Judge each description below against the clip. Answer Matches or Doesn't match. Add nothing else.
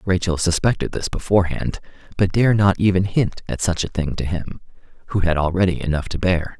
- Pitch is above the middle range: Doesn't match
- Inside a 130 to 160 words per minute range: Doesn't match